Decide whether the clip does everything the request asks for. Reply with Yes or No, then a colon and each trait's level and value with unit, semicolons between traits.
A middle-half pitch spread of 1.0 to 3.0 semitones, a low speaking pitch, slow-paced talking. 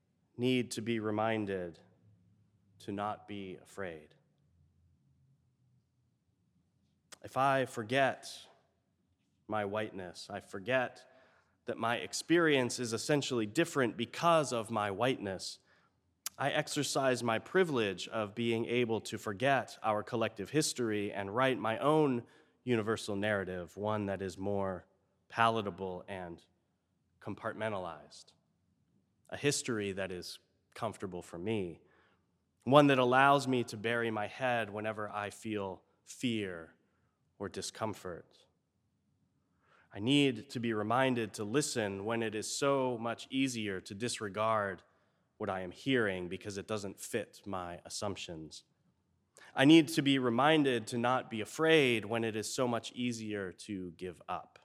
No: average, 4.2 semitones; low, 110 Hz; slow, 125 wpm